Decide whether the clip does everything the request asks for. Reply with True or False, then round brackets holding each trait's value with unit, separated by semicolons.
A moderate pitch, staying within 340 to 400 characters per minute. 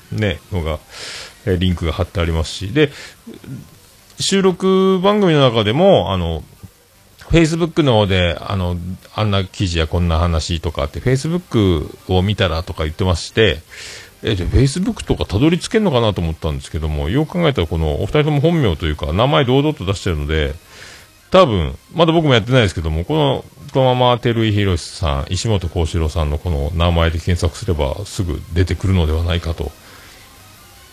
False (95 Hz; 360 characters per minute)